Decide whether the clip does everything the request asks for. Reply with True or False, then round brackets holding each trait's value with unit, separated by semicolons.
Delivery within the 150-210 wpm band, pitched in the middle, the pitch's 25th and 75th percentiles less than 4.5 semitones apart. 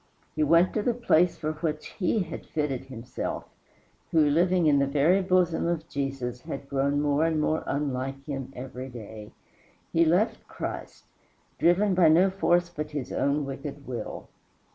True (165 wpm; 150 Hz; 3.9 semitones)